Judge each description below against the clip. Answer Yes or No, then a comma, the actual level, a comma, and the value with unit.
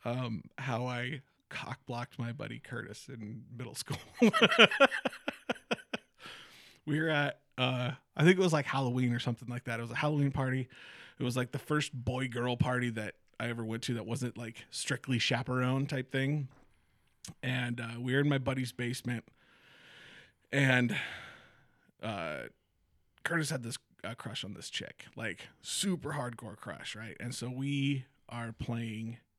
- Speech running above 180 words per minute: No, average, 160 wpm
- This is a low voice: Yes, low, 125 Hz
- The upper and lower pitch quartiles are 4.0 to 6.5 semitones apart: No, average, 2.8 semitones